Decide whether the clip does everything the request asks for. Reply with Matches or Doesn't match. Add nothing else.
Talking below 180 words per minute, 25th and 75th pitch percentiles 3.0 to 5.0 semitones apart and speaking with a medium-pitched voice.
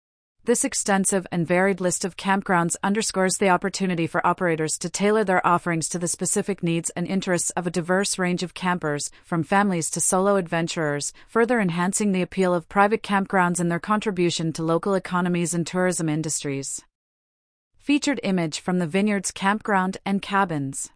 Doesn't match